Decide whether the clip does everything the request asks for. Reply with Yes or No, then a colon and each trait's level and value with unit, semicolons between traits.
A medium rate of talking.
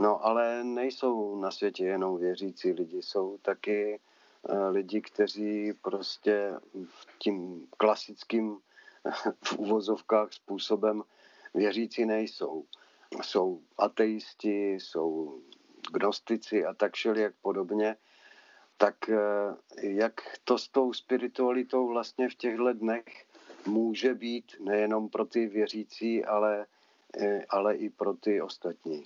No: slow, 105 wpm